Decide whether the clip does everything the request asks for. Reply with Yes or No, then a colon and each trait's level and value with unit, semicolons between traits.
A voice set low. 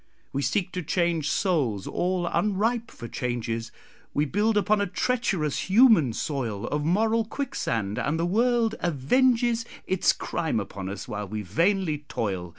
No: medium, 170 Hz